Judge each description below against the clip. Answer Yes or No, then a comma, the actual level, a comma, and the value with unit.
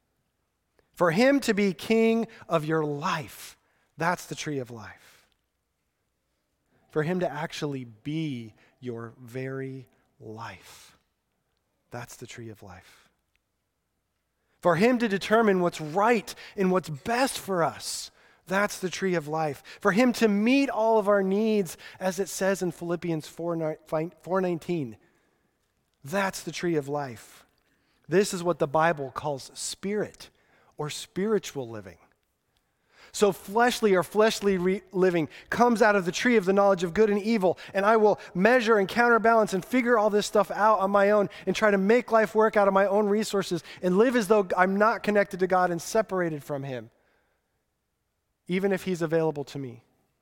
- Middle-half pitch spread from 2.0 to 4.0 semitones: No, average, 5.3 semitones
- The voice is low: No, medium, 185 Hz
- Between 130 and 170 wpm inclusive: Yes, average, 160 wpm